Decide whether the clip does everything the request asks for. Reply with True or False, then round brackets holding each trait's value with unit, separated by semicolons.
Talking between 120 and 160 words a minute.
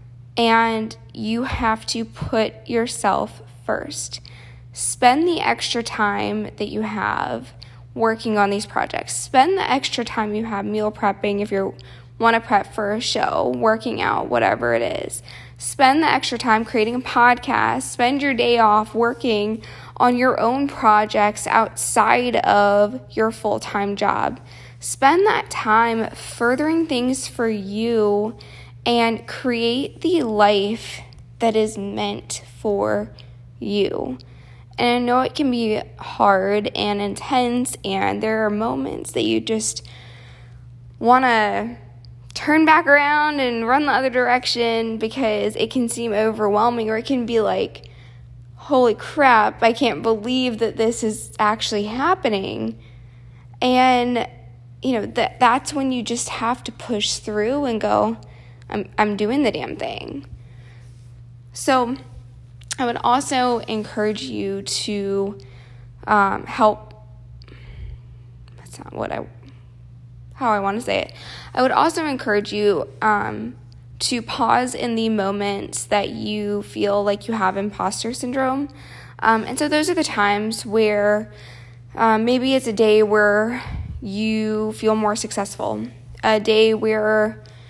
True (140 wpm)